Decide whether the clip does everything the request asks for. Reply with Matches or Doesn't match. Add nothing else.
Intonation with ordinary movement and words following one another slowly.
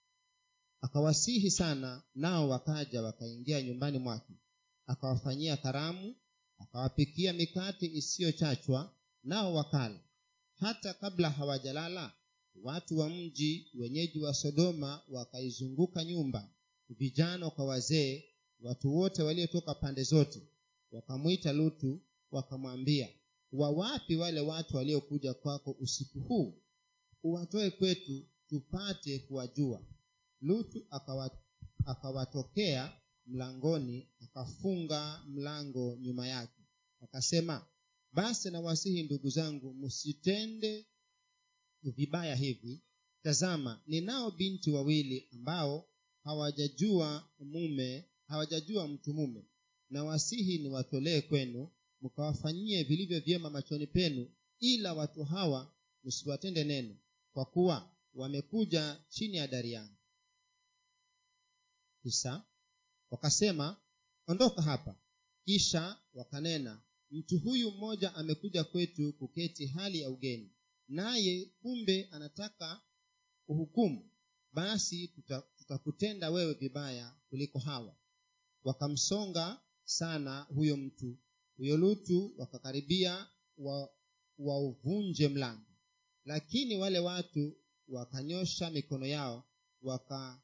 Doesn't match